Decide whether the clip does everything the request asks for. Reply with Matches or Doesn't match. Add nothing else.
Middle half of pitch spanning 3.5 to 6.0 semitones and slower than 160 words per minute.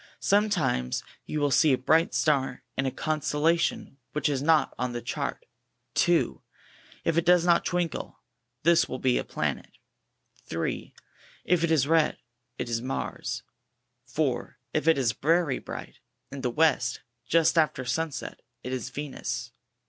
Matches